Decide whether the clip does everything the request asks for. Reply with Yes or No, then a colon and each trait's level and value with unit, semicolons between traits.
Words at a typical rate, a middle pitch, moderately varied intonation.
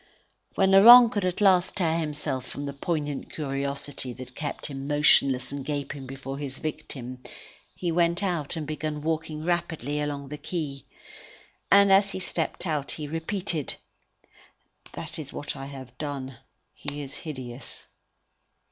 Yes: average, 145 wpm; medium, 150 Hz; average, 3.4 semitones